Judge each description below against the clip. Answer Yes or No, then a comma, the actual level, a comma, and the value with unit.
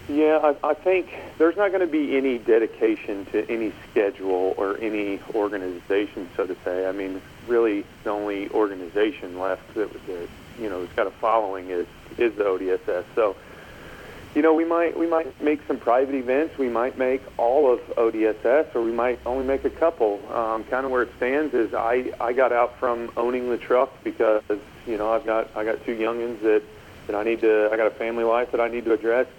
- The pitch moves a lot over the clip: Yes, wide, 5.7 semitones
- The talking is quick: Yes, fast, 210 wpm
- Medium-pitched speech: No, low, 120 Hz